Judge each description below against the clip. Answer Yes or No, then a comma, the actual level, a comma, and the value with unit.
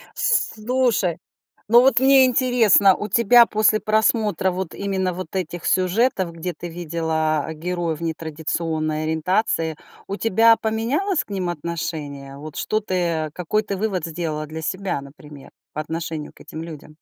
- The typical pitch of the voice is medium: Yes, medium, 180 Hz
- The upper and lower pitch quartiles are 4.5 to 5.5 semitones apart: Yes, average, 5.2 semitones